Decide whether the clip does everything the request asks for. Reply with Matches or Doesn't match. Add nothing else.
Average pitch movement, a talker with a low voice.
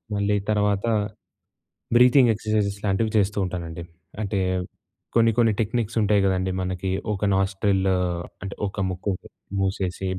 Doesn't match